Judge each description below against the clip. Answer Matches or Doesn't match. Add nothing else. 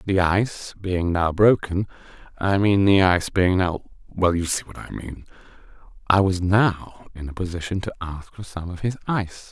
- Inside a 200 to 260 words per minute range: Doesn't match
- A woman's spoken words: Doesn't match